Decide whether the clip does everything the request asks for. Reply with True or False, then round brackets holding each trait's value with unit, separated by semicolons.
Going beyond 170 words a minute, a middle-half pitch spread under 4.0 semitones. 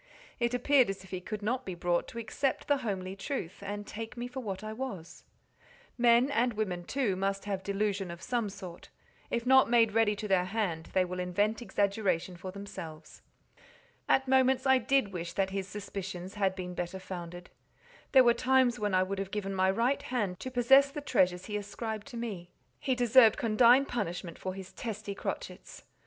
False (190 wpm; 4.4 semitones)